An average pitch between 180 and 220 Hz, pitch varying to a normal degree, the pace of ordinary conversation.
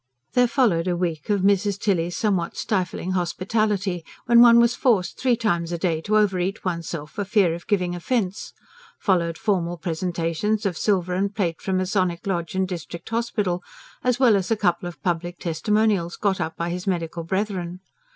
Yes: medium, 185 Hz; average, 3.4 semitones; average, 180 wpm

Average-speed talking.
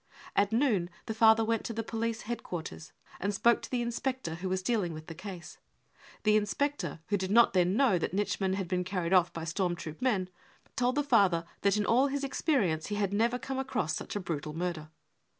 No: fast, 220 wpm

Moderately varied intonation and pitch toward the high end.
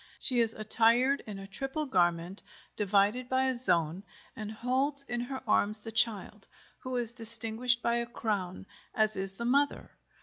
Yes: average, 3.6 semitones; high, 230 Hz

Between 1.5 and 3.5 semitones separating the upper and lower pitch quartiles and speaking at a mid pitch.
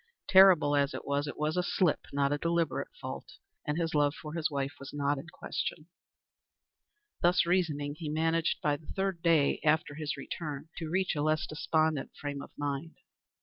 Yes: narrow, 2.5 semitones; medium, 155 Hz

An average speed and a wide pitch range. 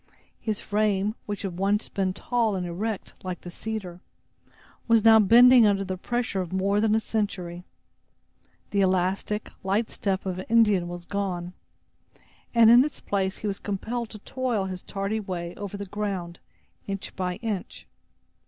No: average, 160 wpm; average, 2.7 semitones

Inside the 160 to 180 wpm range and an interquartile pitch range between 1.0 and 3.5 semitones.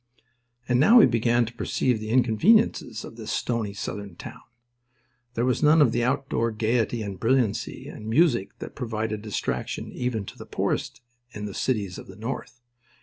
Yes: average, 170 wpm; average, 2.7 semitones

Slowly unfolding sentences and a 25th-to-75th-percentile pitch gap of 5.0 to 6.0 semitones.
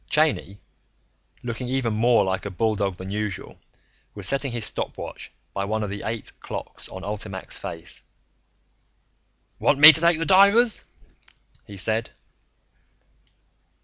Yes: slow, 130 wpm; wide, 5.6 semitones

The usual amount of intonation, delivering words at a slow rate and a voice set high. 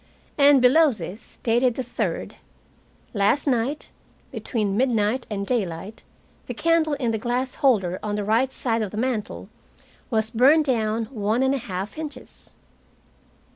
No: average, 3.9 semitones; average, 145 wpm; high, 235 Hz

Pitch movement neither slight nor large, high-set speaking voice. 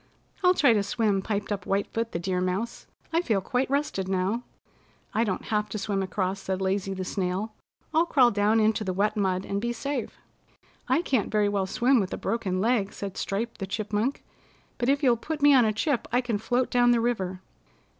Yes: average, 3.8 semitones; high, 215 Hz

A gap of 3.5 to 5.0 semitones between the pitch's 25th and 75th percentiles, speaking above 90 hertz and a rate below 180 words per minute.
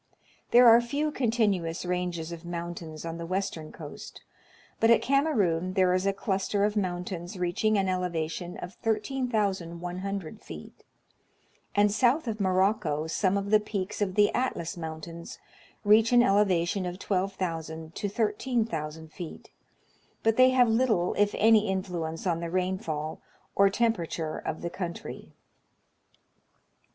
Yes: average, 4.0 semitones; high, 190 Hz; average, 140 wpm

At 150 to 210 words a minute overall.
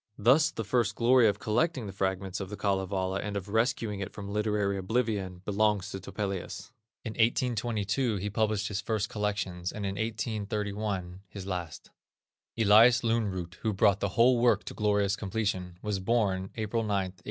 Yes: average, 170 wpm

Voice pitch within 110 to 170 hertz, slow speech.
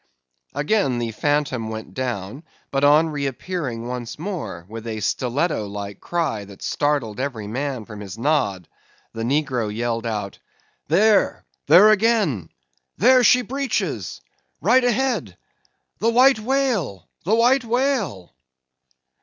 Yes: medium, 140 Hz; slow, 125 wpm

